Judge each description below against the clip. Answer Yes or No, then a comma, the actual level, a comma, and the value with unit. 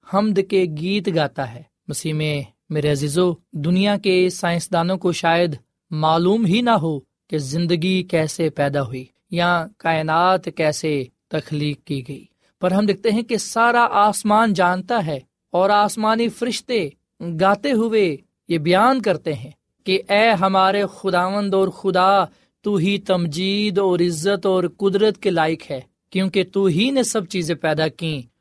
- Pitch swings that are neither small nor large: Yes, average, 4.2 semitones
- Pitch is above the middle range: No, medium, 180 Hz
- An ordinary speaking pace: Yes, average, 150 wpm